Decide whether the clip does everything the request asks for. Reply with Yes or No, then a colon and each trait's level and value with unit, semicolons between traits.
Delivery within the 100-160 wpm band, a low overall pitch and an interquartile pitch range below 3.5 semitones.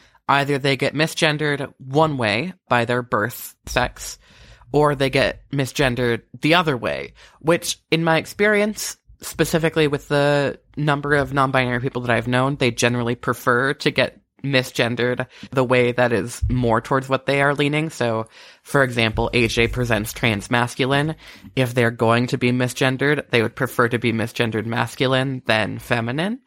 Yes: average, 155 wpm; low, 130 Hz; average, 3.1 semitones